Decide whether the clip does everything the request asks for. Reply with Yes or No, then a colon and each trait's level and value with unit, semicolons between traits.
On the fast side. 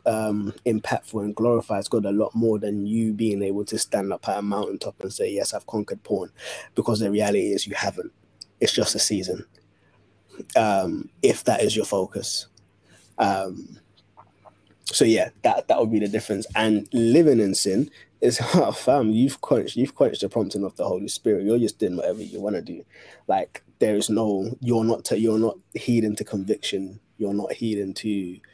No: average, 190 wpm